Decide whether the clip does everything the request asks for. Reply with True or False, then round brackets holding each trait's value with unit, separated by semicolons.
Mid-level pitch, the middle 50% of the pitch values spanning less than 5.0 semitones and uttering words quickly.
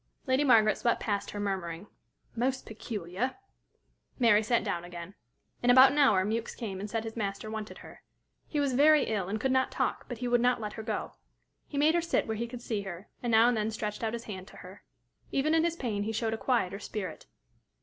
False (220 Hz; 3.5 semitones; 225 wpm)